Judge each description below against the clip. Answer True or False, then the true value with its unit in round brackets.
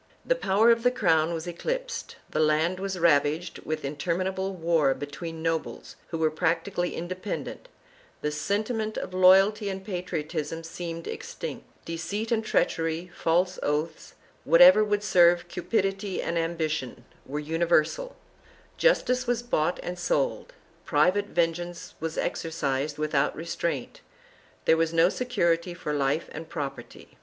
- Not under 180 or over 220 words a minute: False (140 wpm)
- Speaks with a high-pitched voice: False (170 Hz)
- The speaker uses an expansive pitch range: False (3.5 semitones)